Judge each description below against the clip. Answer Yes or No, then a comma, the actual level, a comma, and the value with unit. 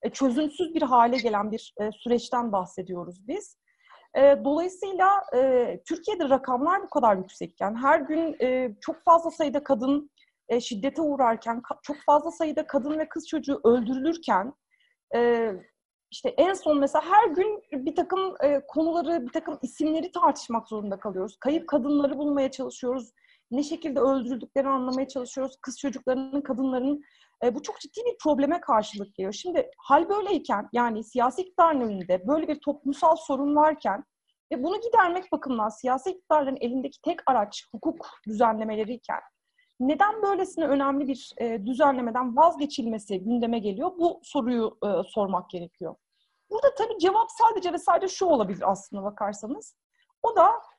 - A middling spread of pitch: No, wide, 5.7 semitones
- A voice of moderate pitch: No, very high, 280 Hz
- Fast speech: Yes, fast, 145 wpm